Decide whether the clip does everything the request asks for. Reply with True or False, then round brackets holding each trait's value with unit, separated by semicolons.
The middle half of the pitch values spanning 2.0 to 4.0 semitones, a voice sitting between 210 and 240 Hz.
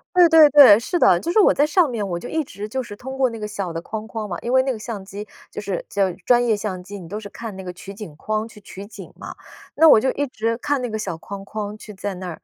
False (4.5 semitones; 215 Hz)